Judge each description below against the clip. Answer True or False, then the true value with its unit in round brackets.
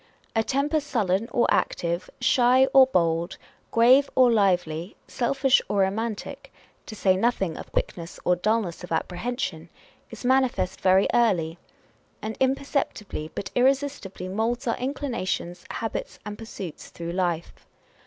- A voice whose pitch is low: False (220 Hz)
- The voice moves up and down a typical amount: False (6.2 semitones)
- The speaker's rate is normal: False (130 wpm)